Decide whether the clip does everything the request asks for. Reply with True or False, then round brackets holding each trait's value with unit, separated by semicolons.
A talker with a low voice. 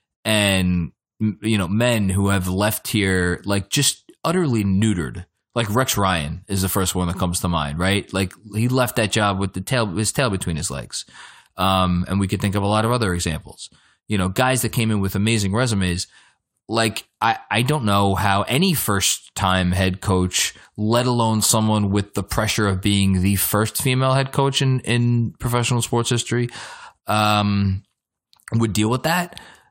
True (105 Hz)